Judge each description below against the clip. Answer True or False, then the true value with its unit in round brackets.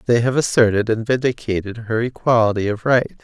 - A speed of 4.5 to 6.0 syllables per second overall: True (5.5 syllables/s)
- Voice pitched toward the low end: True (115 Hz)